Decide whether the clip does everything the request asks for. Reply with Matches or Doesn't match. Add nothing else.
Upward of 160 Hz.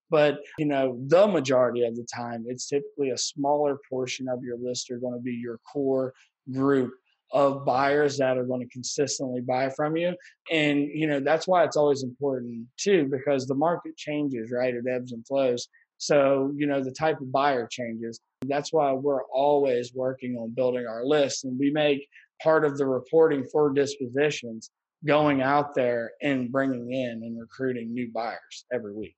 Doesn't match